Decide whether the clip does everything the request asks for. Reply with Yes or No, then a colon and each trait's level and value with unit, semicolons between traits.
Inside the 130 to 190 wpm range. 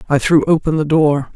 No: fast, 220 wpm